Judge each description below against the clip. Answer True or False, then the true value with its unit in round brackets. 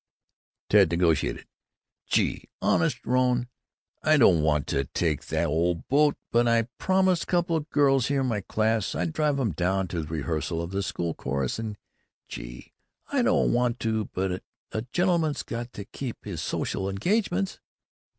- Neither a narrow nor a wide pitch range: False (8.4 semitones)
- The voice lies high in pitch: False (110 Hz)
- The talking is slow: False (160 wpm)